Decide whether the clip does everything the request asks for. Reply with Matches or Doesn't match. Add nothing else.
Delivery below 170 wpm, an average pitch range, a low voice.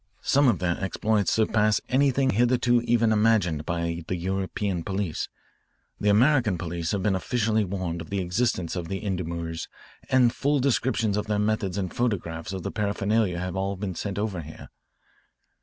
Matches